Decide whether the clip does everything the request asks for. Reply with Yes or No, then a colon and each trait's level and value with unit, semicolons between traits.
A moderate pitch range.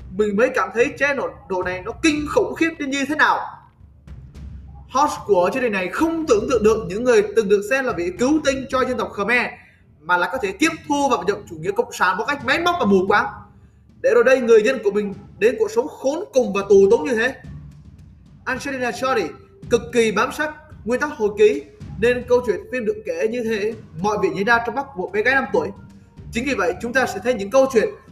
No: wide, 7.9 semitones